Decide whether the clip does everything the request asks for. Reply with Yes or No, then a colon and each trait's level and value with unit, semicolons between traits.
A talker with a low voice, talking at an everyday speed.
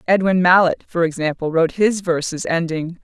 No: medium, 170 Hz; average, 160 wpm